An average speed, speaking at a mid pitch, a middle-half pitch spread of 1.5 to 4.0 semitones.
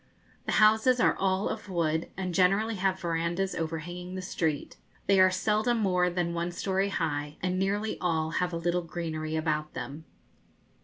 Yes: average, 165 wpm; medium, 180 Hz; average, 2.8 semitones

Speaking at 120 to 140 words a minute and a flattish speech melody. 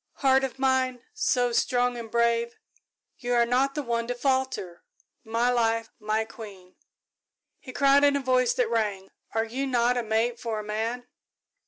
No: average, 170 wpm; narrow, 2.3 semitones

